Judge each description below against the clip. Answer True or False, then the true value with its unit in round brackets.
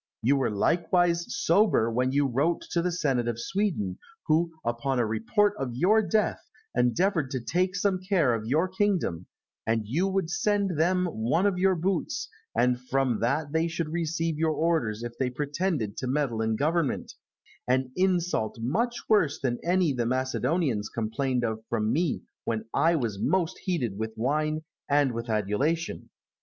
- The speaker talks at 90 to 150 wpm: False (165 wpm)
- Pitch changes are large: True (6.7 semitones)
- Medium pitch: True (145 Hz)